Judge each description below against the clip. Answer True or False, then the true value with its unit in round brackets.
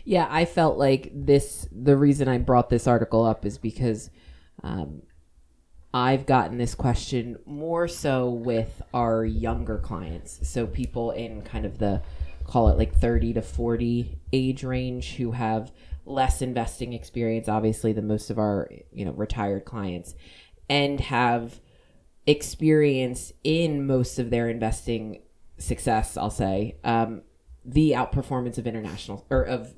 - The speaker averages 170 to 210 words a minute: False (145 wpm)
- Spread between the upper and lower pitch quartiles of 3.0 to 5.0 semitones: True (4.0 semitones)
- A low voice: True (115 Hz)